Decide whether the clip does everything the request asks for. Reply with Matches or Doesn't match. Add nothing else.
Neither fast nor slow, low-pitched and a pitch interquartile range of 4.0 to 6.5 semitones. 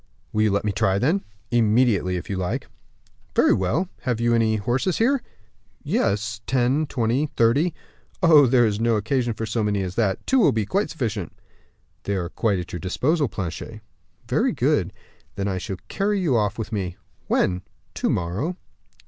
Matches